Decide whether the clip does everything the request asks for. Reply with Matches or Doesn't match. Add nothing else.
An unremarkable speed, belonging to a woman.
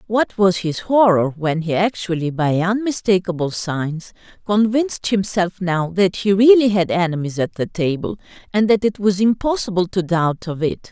Matches